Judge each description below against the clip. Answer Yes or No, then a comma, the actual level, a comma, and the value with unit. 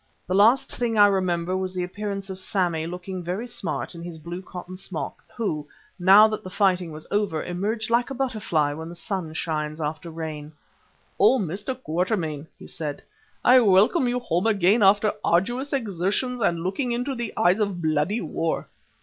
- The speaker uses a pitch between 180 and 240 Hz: Yes, medium, 185 Hz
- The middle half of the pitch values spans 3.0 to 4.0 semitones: No, average, 4.4 semitones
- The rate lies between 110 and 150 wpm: No, average, 175 wpm